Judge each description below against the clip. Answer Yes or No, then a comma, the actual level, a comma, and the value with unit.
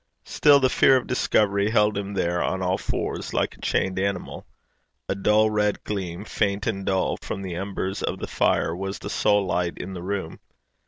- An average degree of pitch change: No, narrow, 1.9 semitones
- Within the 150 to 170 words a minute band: No, average, 195 wpm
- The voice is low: Yes, low, 100 Hz